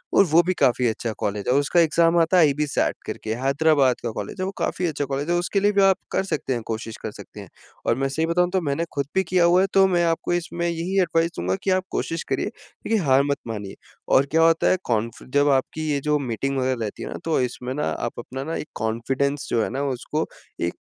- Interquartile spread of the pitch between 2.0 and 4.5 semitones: No, average, 5.1 semitones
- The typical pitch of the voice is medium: Yes, medium, 145 Hz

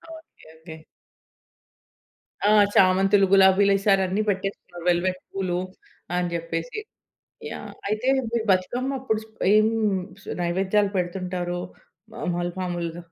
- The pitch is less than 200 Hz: Yes, medium, 185 Hz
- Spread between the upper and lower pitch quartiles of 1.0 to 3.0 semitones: Yes, narrow, 2.5 semitones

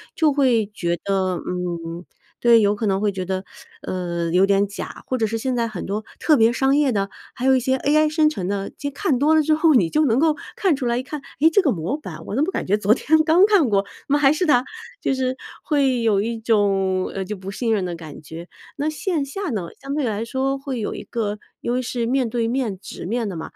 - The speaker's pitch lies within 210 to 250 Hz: Yes, high, 235 Hz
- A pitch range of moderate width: No, wide, 6.2 semitones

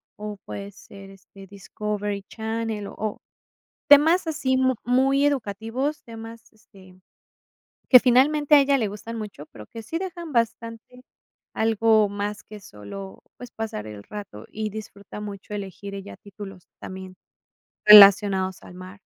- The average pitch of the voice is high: Yes, high, 210 Hz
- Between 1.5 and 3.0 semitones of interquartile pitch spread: No, average, 3.4 semitones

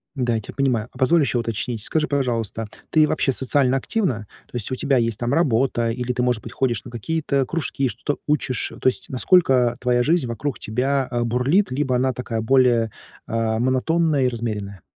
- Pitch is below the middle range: Yes, low, 125 Hz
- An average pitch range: Yes, average, 3.0 semitones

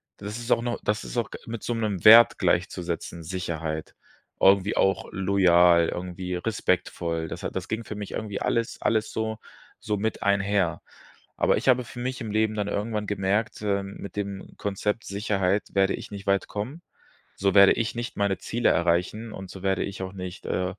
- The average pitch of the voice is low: Yes, low, 100 Hz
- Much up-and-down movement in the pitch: No, average, 2.7 semitones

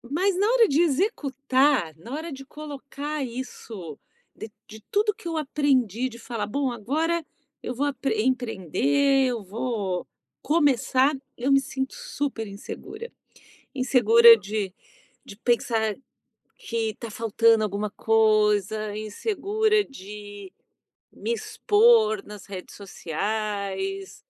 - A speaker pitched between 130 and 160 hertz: No, very high, 250 Hz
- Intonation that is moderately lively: No, wide, 5.8 semitones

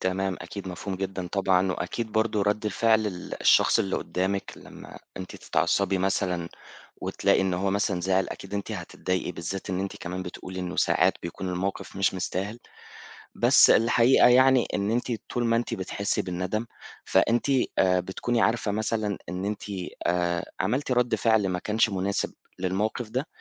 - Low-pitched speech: Yes, very low, 95 Hz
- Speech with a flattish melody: No, average, 3.1 semitones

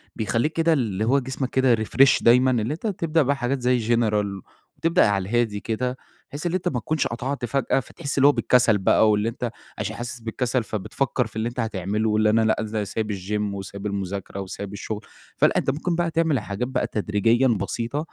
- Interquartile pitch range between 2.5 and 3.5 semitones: No, average, 4.0 semitones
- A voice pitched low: Yes, low, 115 Hz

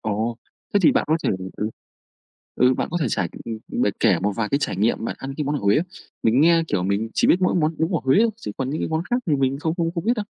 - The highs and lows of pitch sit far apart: Yes, wide, 6.9 semitones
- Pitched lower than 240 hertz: Yes, medium, 140 Hz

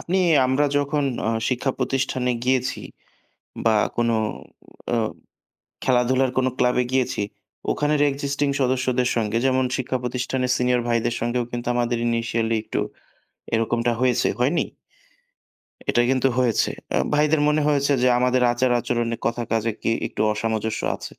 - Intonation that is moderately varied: No, narrow, 1.9 semitones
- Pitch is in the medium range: No, low, 125 Hz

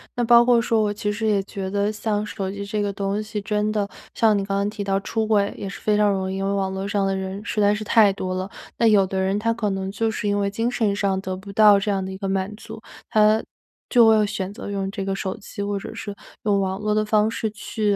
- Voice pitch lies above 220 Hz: No, high, 205 Hz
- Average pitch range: No, narrow, 1.6 semitones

